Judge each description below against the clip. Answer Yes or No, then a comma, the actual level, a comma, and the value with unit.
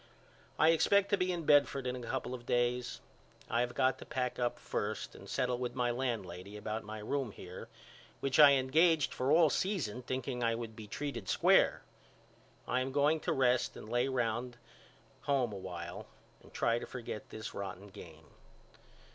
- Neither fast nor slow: Yes, average, 180 wpm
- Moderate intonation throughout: Yes, average, 3.8 semitones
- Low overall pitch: Yes, low, 125 Hz